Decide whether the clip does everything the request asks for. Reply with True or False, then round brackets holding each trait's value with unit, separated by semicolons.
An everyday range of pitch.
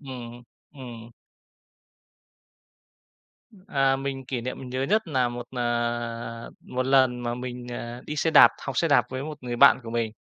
False (2.1 semitones)